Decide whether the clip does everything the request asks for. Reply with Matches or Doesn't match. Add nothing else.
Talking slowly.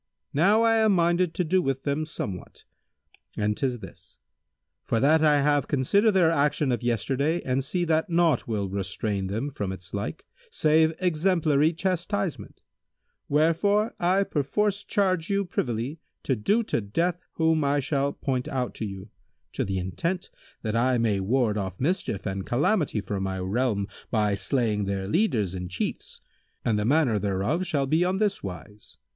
Doesn't match